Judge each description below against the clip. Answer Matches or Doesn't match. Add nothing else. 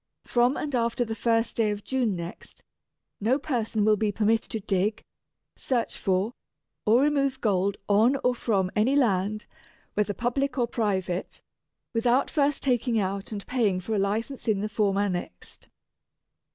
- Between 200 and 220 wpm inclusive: Doesn't match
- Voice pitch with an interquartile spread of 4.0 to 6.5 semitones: Doesn't match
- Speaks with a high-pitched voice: Matches